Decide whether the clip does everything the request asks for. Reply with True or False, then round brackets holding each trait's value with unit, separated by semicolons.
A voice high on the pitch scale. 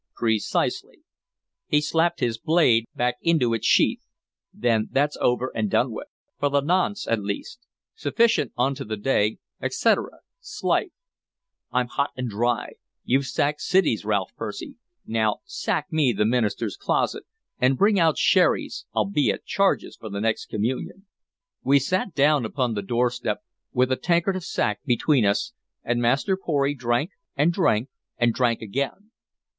False (130 Hz)